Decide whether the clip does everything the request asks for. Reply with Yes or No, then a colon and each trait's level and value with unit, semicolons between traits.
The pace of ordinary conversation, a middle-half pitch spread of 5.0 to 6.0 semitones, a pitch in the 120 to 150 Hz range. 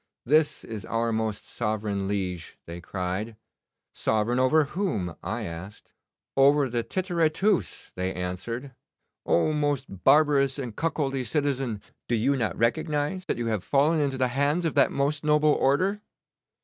Yes: average, 150 wpm; wide, 5.5 semitones; low, 135 Hz